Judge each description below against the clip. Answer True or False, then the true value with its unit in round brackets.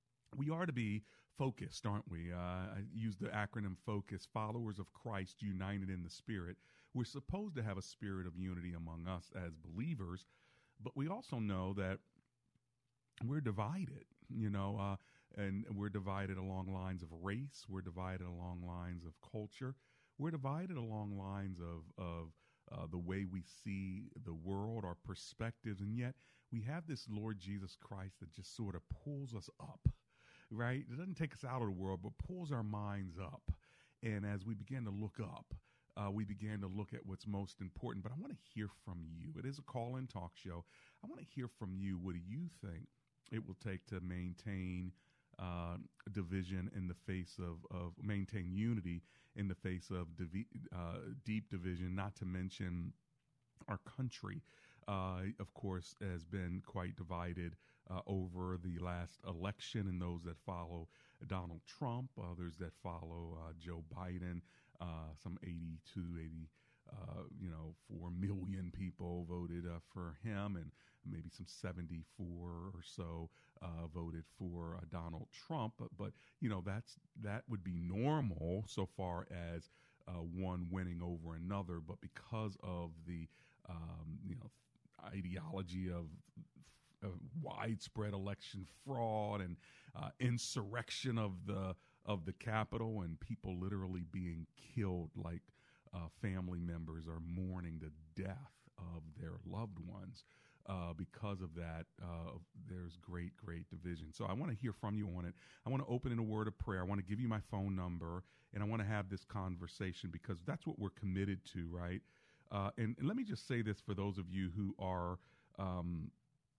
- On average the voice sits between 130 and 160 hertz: False (95 Hz)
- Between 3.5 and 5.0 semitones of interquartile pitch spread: True (3.8 semitones)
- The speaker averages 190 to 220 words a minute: False (175 wpm)